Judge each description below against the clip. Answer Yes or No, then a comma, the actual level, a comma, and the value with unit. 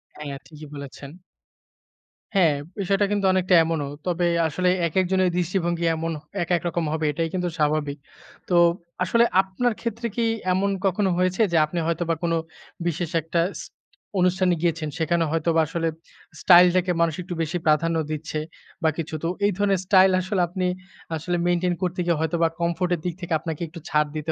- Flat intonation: Yes, narrow, 2.3 semitones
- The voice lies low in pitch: No, medium, 170 Hz